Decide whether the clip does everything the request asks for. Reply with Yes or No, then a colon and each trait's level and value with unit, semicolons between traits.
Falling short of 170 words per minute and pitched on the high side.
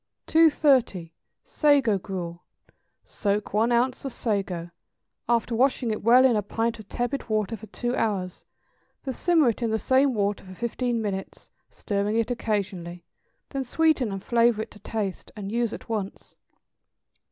Yes: average, 155 wpm; high, 225 Hz